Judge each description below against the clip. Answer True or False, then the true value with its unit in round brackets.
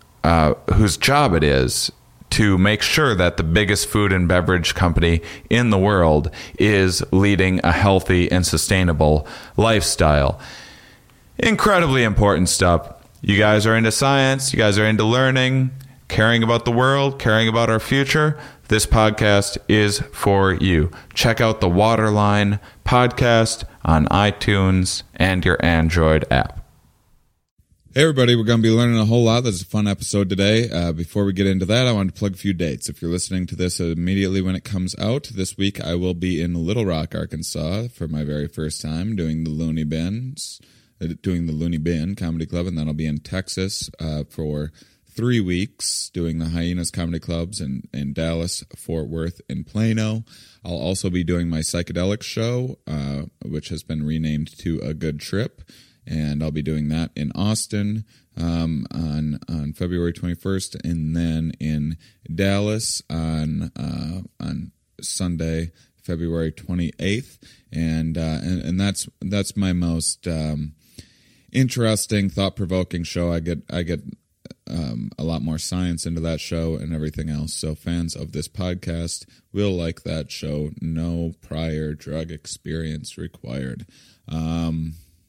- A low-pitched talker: True (90 Hz)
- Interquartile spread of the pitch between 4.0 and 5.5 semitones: True (4.5 semitones)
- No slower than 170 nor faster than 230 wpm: False (160 wpm)